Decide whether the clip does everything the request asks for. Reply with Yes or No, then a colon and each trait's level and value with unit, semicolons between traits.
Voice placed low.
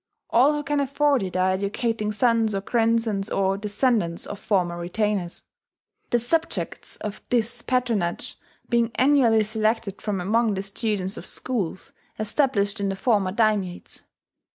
No: high, 215 Hz